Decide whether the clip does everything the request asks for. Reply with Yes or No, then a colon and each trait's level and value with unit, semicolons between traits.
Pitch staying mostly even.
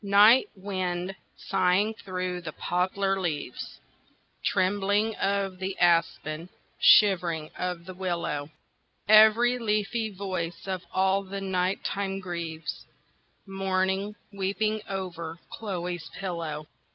Yes: narrow, 2.2 semitones